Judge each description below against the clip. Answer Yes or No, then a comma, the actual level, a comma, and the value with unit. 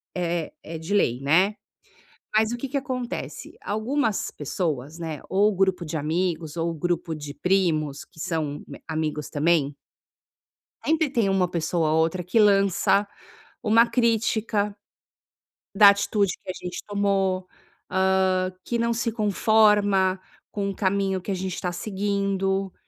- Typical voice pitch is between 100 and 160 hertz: No, high, 190 Hz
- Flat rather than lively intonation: No, average, 3.7 semitones